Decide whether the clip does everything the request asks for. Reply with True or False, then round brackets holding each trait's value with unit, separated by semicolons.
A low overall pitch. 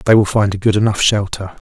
True (100 Hz)